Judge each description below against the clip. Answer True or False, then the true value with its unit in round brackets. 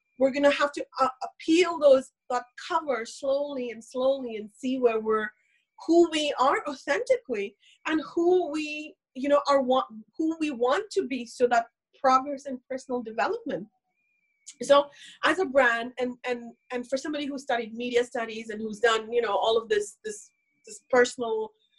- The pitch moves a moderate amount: True (4.1 semitones)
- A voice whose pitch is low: False (265 Hz)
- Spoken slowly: False (175 wpm)